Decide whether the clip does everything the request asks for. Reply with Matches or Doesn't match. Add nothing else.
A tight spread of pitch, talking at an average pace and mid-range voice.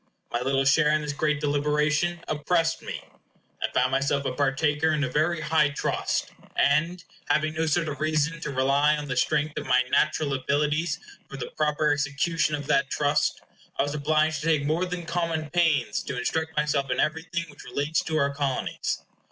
Matches